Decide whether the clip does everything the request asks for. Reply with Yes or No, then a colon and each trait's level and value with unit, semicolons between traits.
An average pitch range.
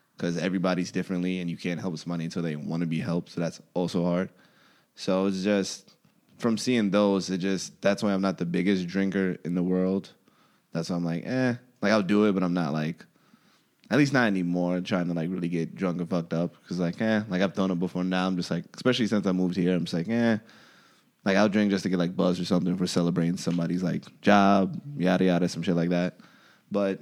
No: narrow, 2.1 semitones